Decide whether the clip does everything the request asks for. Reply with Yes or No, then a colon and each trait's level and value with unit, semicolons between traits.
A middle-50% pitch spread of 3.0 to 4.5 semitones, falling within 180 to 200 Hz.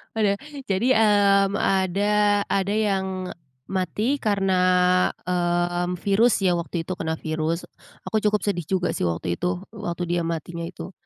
No: narrow, 2.6 semitones; medium, 185 Hz